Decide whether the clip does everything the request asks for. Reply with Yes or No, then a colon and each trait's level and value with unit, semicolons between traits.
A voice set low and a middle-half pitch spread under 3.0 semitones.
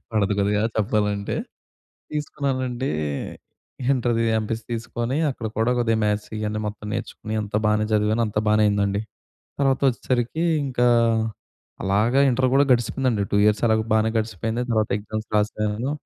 Yes: low, 110 Hz; narrow, 2.6 semitones